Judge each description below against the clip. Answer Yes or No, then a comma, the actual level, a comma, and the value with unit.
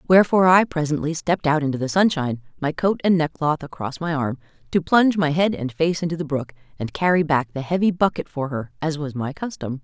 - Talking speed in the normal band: No, fast, 220 wpm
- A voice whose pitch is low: No, medium, 155 Hz